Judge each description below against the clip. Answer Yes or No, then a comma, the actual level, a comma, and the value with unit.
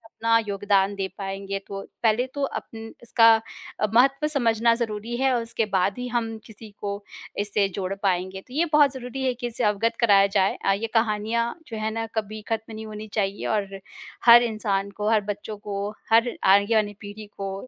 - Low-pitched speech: No, high, 215 Hz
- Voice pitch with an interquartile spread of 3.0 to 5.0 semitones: No, narrow, 2.6 semitones